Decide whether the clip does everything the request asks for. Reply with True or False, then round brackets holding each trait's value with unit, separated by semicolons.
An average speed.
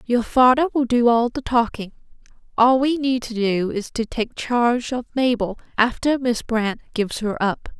True (185 wpm)